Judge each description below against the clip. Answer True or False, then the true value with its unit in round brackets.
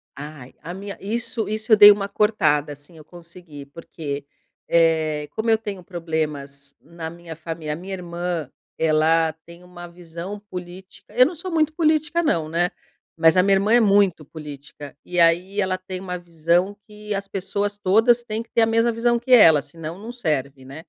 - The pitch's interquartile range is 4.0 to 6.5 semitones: True (4.6 semitones)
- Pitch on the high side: False (175 Hz)